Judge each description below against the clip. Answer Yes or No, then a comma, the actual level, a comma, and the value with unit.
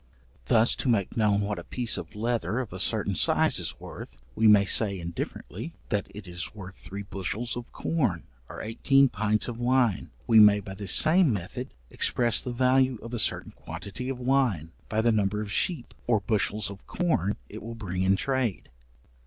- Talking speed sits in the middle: Yes, average, 190 wpm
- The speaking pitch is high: No, low, 110 Hz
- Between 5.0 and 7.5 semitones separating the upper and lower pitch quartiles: No, average, 3.6 semitones